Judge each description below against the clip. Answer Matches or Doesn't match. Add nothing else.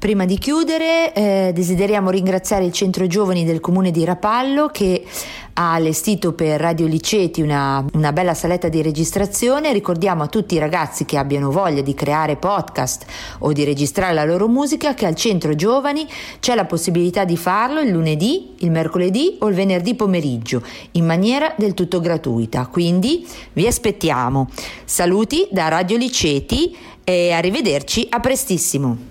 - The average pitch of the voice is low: Doesn't match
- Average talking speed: Matches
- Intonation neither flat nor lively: Matches